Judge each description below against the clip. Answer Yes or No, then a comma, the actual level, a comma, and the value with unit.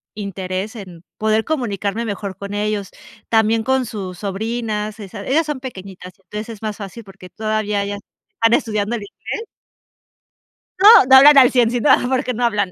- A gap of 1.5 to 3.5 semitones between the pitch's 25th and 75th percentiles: Yes, average, 2.9 semitones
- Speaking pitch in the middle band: No, high, 215 Hz